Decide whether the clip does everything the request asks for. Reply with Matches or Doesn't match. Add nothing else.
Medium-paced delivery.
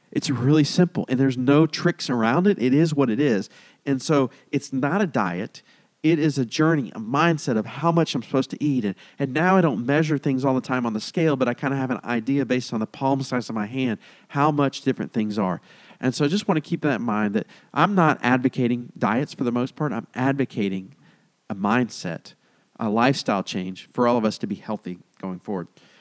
Doesn't match